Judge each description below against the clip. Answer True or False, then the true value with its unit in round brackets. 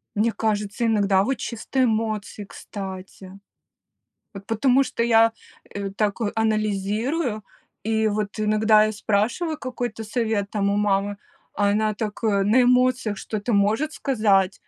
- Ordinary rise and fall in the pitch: False (2.1 semitones)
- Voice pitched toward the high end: True (215 Hz)